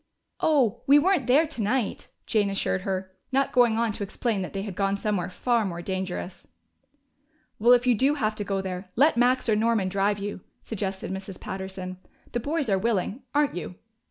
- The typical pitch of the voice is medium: No, high, 210 Hz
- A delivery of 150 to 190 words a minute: Yes, average, 185 wpm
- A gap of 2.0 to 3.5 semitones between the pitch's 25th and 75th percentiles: No, average, 4.3 semitones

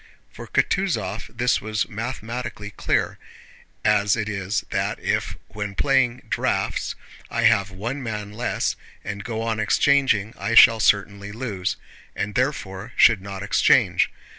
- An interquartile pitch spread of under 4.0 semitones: Yes, average, 2.7 semitones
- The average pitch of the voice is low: Yes, low, 110 Hz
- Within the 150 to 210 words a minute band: No, slow, 135 wpm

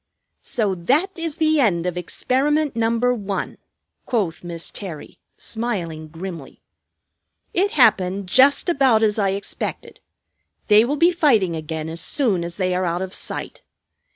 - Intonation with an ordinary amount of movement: No, wide, 7.2 semitones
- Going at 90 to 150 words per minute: Yes, average, 145 wpm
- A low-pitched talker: No, high, 205 Hz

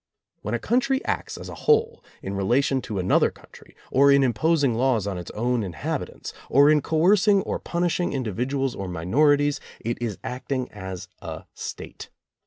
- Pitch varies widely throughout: Yes, wide, 6.4 semitones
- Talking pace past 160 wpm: Yes, average, 175 wpm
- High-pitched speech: No, low, 130 Hz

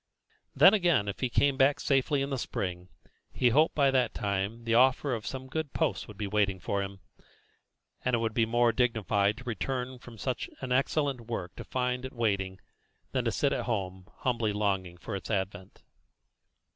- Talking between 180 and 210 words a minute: Yes, average, 190 wpm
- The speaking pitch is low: Yes, low, 115 Hz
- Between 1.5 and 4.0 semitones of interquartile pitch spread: No, average, 4.5 semitones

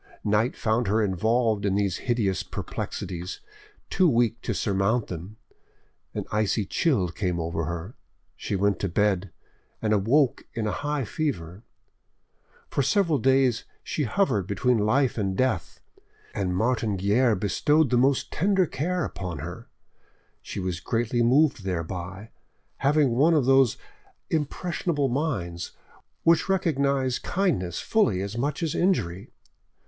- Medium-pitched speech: No, low, 115 Hz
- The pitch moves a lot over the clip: Yes, wide, 6.5 semitones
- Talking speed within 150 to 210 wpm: No, slow, 135 wpm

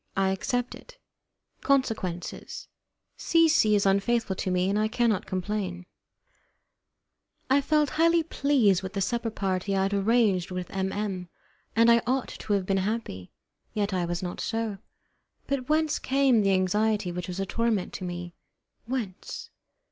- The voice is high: Yes, high, 205 Hz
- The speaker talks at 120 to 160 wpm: Yes, average, 155 wpm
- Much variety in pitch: No, average, 4.2 semitones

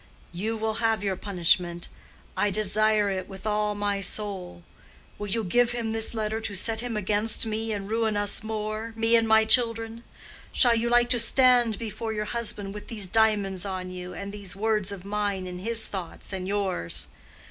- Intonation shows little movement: Yes, narrow, 2.3 semitones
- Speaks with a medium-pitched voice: No, high, 210 Hz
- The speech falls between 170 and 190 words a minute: Yes, average, 180 wpm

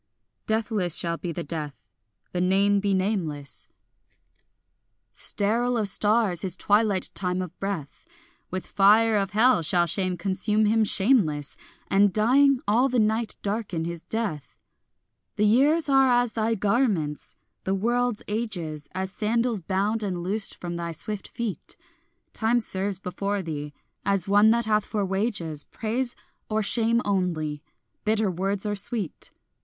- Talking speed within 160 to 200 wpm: No, average, 140 wpm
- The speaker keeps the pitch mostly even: No, average, 3.6 semitones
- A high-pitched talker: Yes, high, 200 Hz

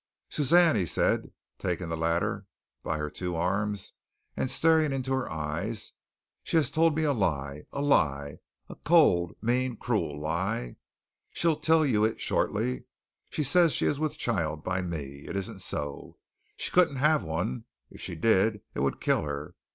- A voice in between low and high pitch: No, low, 100 Hz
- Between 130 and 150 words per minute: No, average, 165 wpm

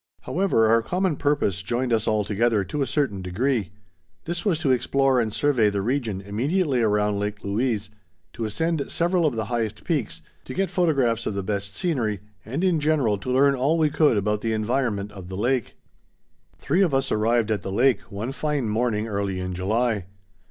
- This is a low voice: Yes, low, 115 Hz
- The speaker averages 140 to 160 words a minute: No, average, 190 wpm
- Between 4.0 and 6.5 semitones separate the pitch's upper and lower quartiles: Yes, average, 5.2 semitones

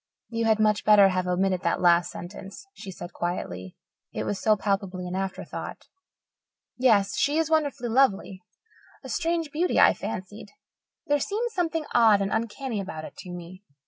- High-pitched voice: Yes, high, 205 Hz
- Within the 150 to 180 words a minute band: Yes, average, 170 wpm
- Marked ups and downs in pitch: Yes, wide, 6.6 semitones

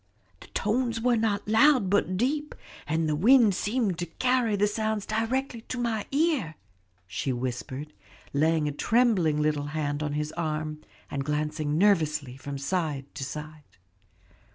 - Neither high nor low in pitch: Yes, medium, 165 Hz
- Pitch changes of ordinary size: No, wide, 7.0 semitones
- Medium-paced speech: Yes, average, 150 wpm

